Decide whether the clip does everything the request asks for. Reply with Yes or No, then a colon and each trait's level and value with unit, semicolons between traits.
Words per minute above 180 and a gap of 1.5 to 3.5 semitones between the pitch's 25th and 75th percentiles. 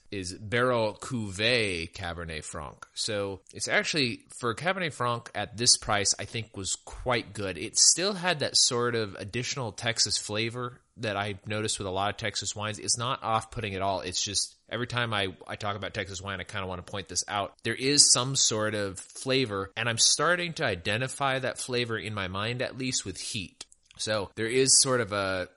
No: fast, 205 wpm; average, 4.0 semitones